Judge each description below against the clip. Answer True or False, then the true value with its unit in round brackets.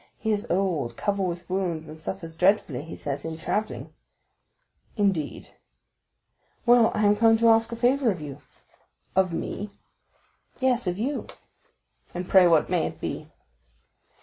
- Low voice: False (190 Hz)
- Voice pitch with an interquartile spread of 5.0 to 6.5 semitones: True (5.3 semitones)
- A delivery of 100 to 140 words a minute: False (150 wpm)